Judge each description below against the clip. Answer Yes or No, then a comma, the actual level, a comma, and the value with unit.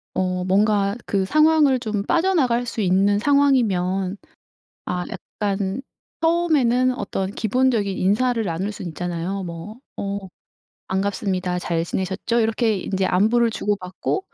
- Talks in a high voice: Yes, high, 205 Hz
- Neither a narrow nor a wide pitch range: Yes, average, 4.3 semitones